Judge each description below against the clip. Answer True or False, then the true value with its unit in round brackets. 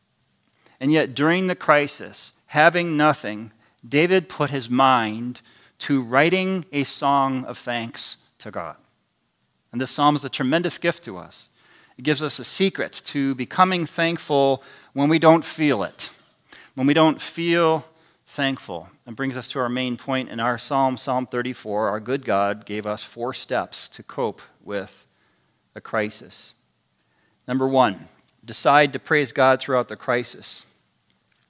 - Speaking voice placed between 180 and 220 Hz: False (135 Hz)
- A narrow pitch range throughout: False (3.7 semitones)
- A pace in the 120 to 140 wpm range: False (150 wpm)